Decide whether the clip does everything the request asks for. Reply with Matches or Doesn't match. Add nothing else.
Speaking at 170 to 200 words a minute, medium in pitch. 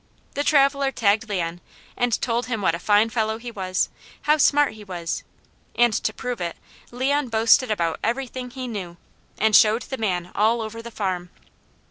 Doesn't match